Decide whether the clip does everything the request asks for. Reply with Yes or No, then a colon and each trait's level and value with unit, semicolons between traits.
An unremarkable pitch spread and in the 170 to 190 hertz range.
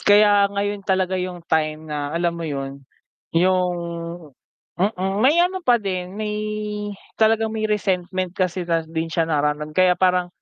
Yes: average, 3.6 semitones; medium, 185 Hz